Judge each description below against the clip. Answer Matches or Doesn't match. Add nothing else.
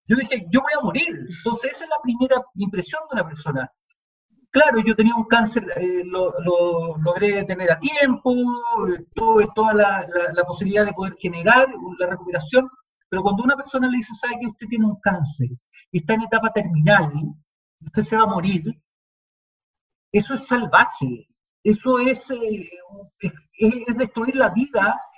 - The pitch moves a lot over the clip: Matches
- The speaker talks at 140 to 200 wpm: Matches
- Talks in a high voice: Matches